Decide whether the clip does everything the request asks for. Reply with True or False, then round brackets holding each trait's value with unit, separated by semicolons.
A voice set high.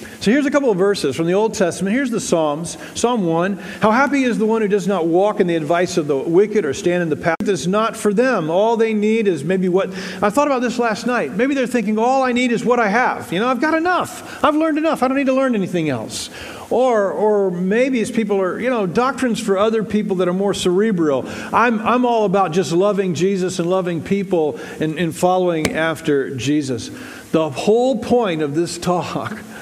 True (200 Hz)